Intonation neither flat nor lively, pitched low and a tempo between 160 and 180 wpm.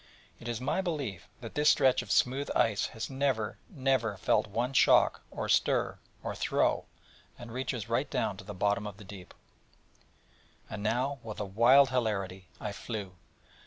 Yes: average, 4.2 semitones; low, 115 Hz; average, 165 wpm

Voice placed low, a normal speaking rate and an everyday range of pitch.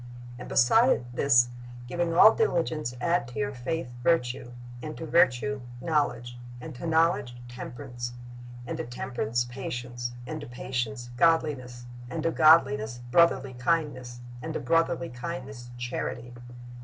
No: low, 130 Hz; slow, 130 wpm; average, 4.9 semitones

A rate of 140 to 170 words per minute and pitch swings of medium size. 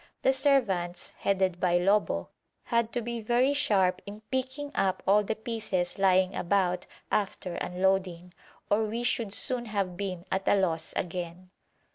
Yes: average, 150 wpm; average, 4.1 semitones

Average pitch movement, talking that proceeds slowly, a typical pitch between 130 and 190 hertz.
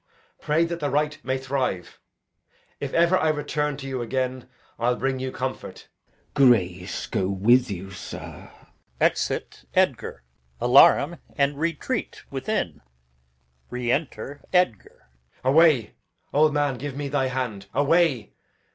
Yes: average, 3.3 semitones; slow, 130 wpm; low, 135 Hz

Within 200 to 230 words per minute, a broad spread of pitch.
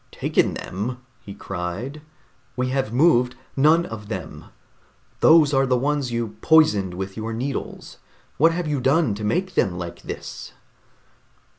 No: average, 145 wpm; wide, 5.9 semitones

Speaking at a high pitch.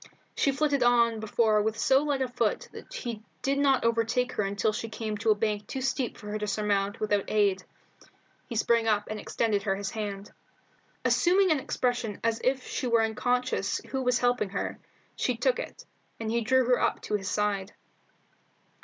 Yes: high, 225 Hz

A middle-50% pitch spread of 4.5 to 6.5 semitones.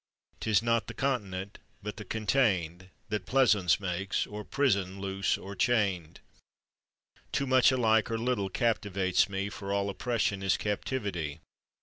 No: average, 3.3 semitones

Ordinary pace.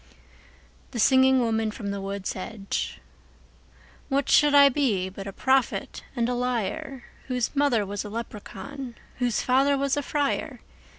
Yes: average, 145 wpm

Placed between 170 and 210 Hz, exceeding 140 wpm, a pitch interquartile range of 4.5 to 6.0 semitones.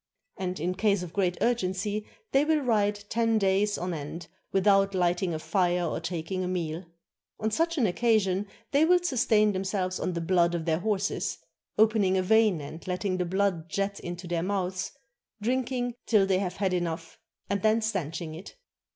No: high, 190 Hz; average, 175 wpm; average, 3.3 semitones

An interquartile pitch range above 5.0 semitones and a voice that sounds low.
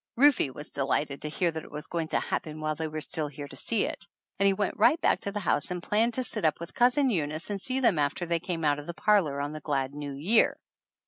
No: wide, 5.6 semitones; medium, 160 Hz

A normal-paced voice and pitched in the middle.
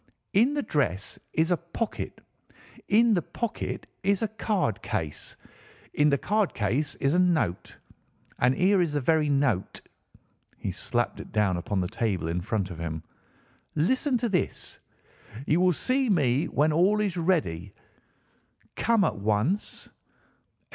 Yes: average, 150 wpm; medium, 155 Hz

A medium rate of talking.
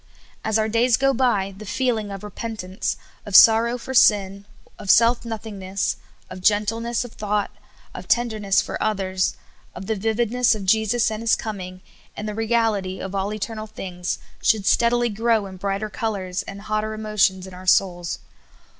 Yes: average, 165 wpm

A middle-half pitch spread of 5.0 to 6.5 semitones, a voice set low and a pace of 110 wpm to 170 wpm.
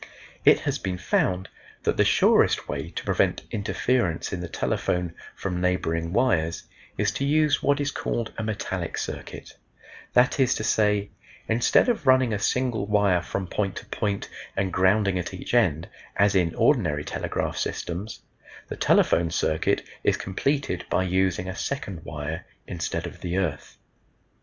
No: average, 4.4 semitones; very low, 95 Hz; average, 155 wpm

